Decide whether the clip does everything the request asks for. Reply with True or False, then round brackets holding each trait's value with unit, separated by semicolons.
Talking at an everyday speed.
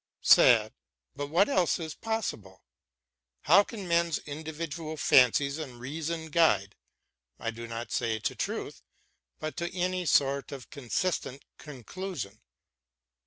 False (120 wpm)